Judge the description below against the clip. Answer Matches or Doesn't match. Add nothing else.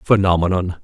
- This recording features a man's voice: Matches